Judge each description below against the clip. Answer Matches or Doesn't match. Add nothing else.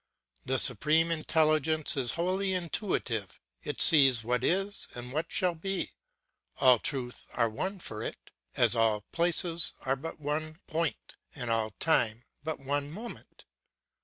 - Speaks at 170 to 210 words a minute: Doesn't match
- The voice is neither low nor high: Matches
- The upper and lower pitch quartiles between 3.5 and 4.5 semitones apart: Doesn't match